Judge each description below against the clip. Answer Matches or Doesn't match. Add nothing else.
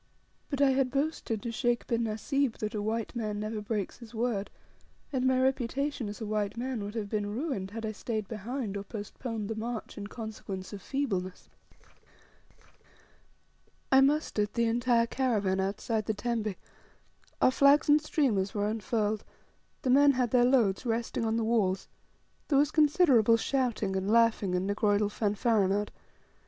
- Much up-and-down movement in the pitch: Doesn't match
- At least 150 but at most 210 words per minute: Matches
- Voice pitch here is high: Matches